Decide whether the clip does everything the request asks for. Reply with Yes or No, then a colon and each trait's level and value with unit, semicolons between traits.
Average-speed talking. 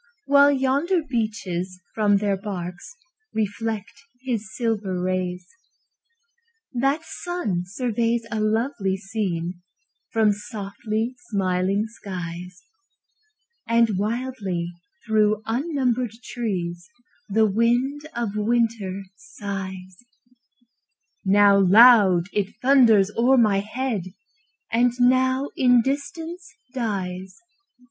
No: slow, 90 wpm